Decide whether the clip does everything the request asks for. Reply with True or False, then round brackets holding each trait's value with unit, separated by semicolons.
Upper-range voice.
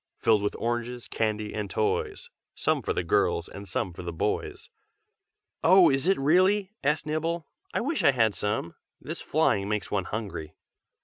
False (115 Hz)